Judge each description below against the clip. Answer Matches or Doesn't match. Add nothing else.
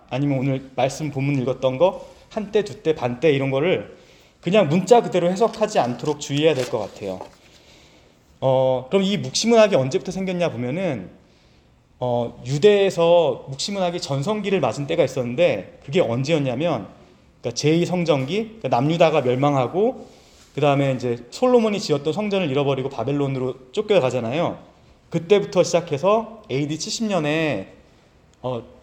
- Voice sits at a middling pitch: Matches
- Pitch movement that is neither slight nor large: Doesn't match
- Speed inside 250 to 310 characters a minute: Doesn't match